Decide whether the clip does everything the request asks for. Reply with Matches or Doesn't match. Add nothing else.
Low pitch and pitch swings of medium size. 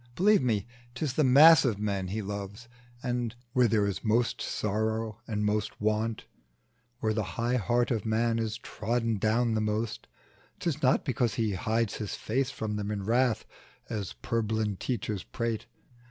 Doesn't match